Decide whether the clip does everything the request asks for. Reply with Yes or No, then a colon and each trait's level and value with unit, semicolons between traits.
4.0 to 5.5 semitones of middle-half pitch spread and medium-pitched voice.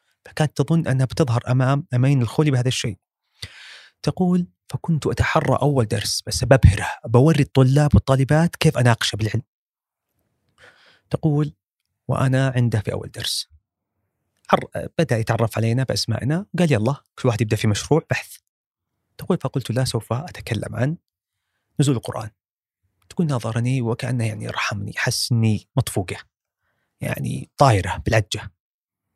No: average, 4.5 semitones; low, 120 Hz